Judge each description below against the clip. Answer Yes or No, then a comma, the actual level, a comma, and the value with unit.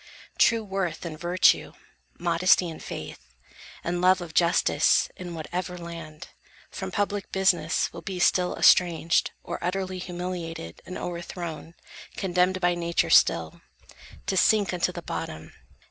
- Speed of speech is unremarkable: No, slow, 130 wpm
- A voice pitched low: No, medium, 175 Hz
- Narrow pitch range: Yes, narrow, 1.6 semitones